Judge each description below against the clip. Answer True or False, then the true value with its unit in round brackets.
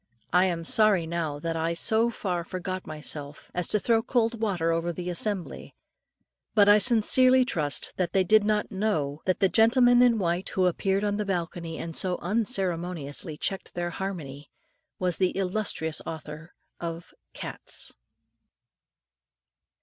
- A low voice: False (180 Hz)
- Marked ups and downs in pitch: False (4.2 semitones)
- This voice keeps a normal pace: True (150 wpm)